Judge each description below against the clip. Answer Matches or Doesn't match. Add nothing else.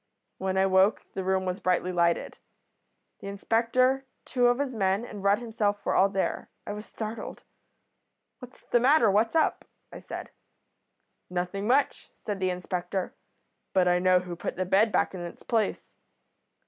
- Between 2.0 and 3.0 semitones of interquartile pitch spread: Doesn't match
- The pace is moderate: Matches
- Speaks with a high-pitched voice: Matches